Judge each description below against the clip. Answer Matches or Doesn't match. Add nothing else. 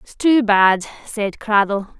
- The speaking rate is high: Doesn't match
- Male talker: Doesn't match